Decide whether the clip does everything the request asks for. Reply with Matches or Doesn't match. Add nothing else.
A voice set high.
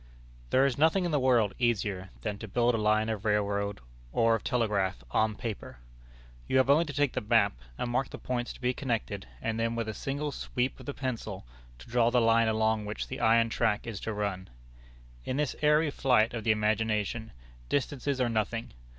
Doesn't match